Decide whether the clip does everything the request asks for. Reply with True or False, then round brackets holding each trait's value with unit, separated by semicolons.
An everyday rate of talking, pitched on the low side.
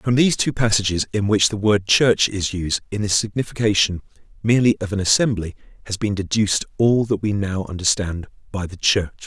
True (190 wpm; 105 Hz)